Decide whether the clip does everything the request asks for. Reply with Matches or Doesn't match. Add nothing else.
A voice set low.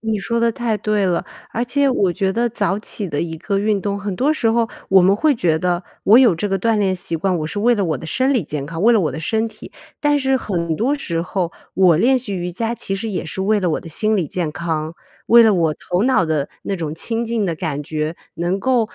Doesn't match